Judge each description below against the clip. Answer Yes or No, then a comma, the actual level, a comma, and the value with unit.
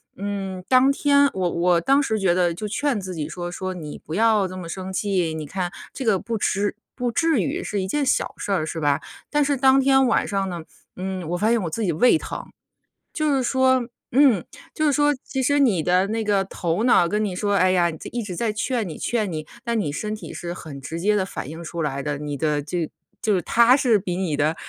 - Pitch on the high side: Yes, high, 195 Hz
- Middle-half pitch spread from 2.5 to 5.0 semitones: No, wide, 5.6 semitones